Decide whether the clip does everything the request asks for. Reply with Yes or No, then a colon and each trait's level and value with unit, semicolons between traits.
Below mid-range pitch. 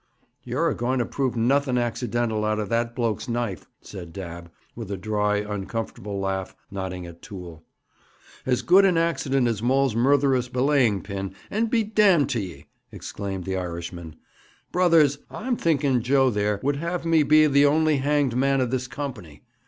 Yes: low, 120 Hz